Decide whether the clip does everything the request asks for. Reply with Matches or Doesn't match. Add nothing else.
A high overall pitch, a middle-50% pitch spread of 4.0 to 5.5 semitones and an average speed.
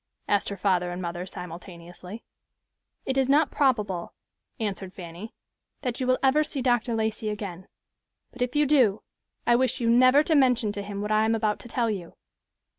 Matches